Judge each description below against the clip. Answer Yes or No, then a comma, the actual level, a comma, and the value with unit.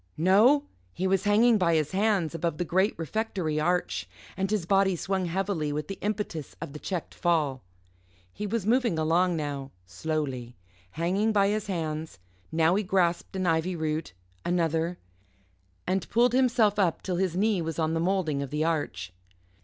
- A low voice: No, medium, 175 Hz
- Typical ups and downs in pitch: Yes, average, 3.8 semitones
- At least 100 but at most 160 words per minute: No, average, 170 wpm